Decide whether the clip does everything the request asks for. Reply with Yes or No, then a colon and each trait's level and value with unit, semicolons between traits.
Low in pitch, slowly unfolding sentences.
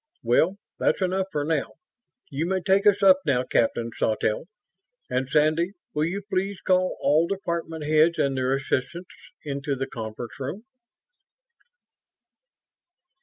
No: medium, 155 Hz; slow, 130 wpm